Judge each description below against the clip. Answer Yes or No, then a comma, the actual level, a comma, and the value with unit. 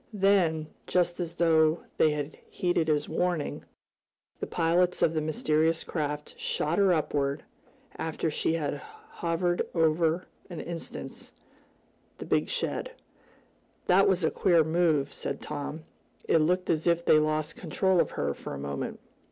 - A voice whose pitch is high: No, medium, 160 Hz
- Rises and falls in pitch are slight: Yes, narrow, 2.3 semitones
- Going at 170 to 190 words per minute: No, average, 150 wpm